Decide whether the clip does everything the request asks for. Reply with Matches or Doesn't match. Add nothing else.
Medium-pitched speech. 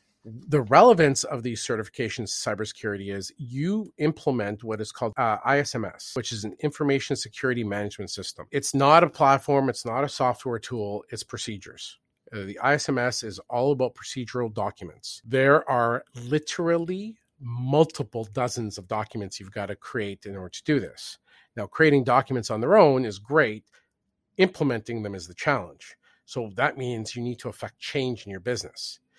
Doesn't match